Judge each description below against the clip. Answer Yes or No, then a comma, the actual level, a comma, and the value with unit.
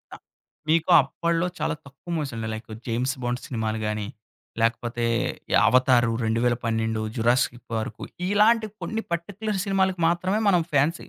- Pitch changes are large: Yes, wide, 7.1 semitones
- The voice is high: No, low, 130 Hz